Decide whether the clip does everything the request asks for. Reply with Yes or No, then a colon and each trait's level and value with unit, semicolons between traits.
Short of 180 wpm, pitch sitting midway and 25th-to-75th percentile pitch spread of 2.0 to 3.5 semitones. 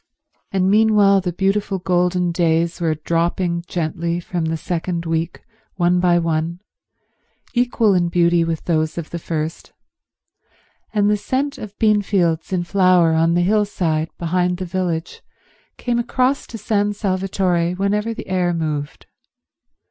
Yes: average, 140 wpm; medium, 180 Hz; average, 2.9 semitones